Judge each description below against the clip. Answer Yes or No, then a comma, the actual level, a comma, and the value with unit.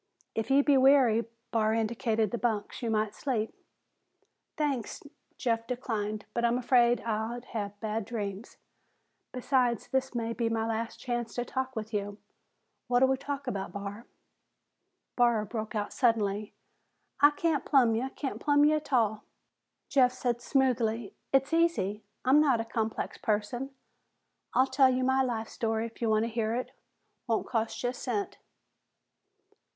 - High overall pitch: Yes, high, 235 Hz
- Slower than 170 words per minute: Yes, average, 155 wpm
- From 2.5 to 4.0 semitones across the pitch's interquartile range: Yes, average, 2.9 semitones